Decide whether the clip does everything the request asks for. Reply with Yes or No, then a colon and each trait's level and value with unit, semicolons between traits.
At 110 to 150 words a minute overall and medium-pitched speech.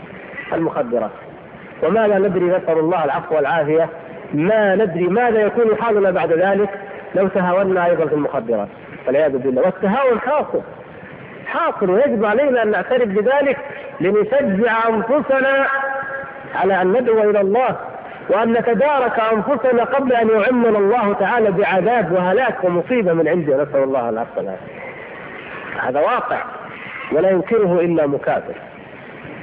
No: average, 120 wpm; high, 210 Hz